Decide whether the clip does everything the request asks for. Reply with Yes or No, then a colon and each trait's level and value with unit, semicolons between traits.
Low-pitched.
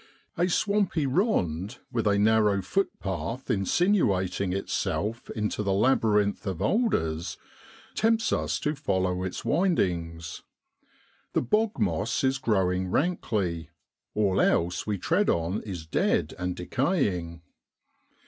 Yes: low, 100 Hz